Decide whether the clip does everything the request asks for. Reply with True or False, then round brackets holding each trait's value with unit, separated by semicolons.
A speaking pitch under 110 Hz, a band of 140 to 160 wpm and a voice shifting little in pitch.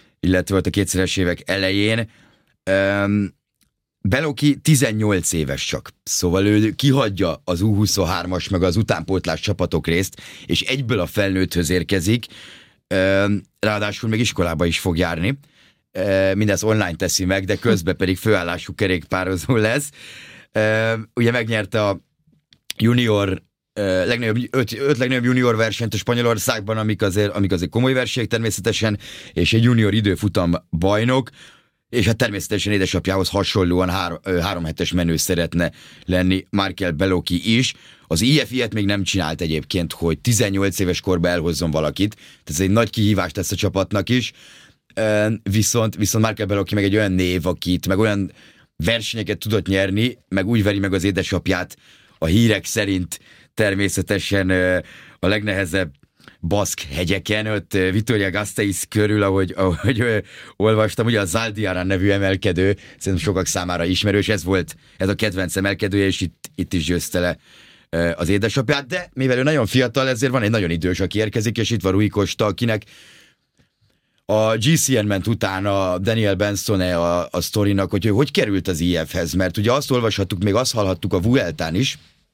False (100 Hz; 150 wpm; 3.2 semitones)